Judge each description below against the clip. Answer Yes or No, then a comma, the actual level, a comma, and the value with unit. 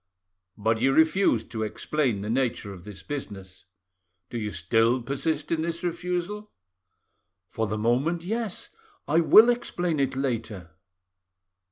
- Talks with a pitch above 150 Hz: No, low, 135 Hz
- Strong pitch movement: Yes, wide, 7.2 semitones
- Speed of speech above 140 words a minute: No, slow, 135 wpm